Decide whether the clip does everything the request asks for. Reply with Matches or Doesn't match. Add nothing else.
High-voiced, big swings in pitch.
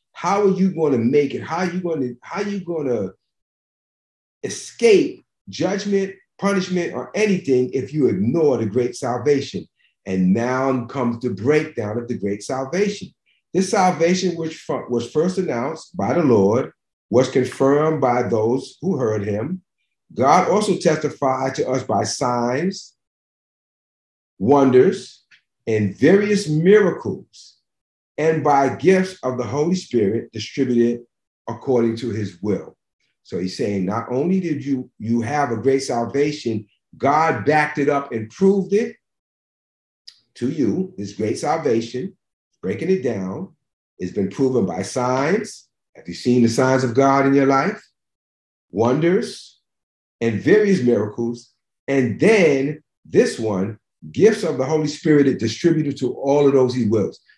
Doesn't match